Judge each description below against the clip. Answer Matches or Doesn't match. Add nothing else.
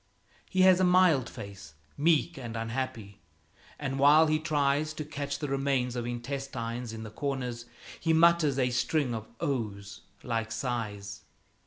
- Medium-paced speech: Matches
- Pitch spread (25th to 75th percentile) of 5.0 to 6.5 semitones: Doesn't match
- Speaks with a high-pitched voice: Doesn't match